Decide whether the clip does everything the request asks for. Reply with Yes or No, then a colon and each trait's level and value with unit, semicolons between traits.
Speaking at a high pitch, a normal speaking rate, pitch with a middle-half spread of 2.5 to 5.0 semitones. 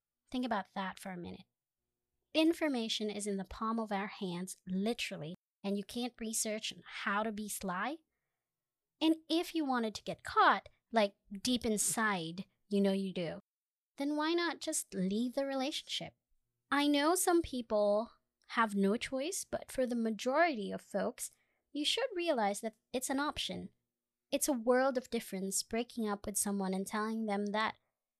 No: high, 225 Hz; average, 165 wpm; wide, 5.5 semitones